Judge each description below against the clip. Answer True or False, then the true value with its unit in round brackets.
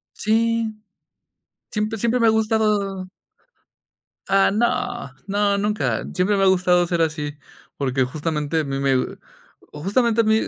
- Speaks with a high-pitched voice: True (200 Hz)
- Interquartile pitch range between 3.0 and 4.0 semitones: False (5.5 semitones)